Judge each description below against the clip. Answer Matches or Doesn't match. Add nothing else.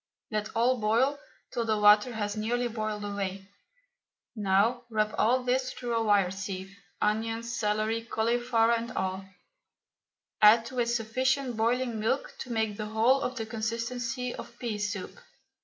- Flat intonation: Matches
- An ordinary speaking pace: Matches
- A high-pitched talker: Matches